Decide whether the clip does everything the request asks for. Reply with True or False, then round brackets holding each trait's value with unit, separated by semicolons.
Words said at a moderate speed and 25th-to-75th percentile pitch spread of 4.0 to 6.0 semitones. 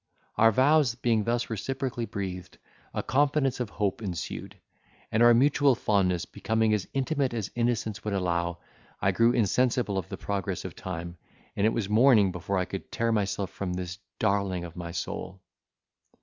True (165 wpm; 4.4 semitones)